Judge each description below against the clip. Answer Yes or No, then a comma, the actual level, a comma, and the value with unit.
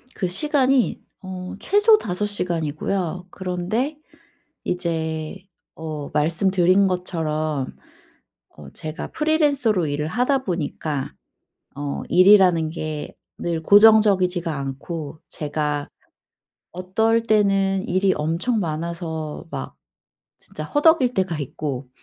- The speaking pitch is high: No, medium, 180 Hz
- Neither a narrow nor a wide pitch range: Yes, average, 4.7 semitones